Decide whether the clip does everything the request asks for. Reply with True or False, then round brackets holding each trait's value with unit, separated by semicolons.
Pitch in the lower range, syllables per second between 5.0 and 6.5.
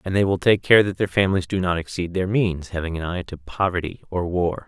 True (90 Hz; 5.8 syllables/s)